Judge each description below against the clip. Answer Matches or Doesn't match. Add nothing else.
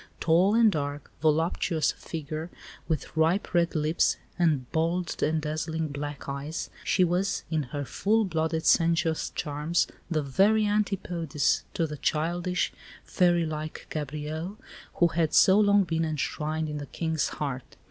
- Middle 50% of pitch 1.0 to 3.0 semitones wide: Matches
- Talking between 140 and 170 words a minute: Matches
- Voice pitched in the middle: Matches